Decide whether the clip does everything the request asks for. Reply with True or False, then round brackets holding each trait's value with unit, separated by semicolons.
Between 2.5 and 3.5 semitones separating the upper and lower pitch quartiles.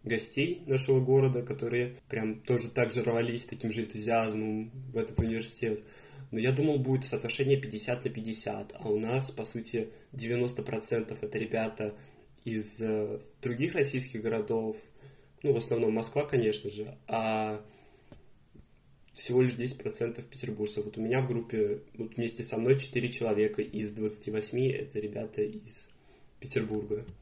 True (2.9 semitones)